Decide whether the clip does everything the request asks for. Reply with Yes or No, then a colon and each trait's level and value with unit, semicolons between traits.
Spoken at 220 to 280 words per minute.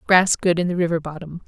Yes: fast, 245 wpm